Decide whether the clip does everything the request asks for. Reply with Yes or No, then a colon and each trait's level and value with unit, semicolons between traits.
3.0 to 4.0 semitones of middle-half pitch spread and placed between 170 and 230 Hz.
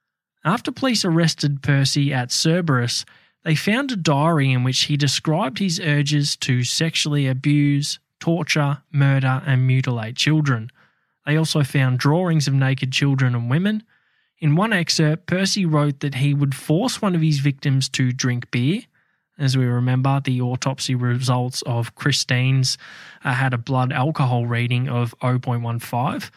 No: average, 3.6 semitones; medium, 140 Hz